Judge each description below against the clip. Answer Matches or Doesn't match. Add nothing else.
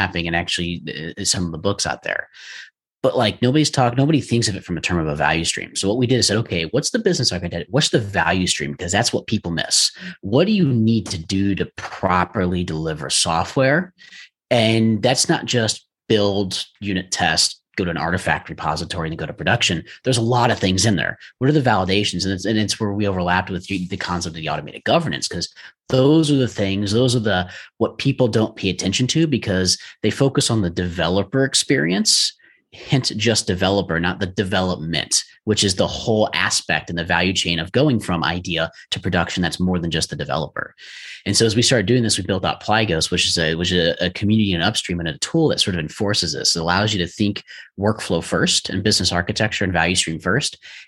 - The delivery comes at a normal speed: Doesn't match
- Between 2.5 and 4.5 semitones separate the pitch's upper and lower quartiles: Doesn't match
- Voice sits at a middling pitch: Doesn't match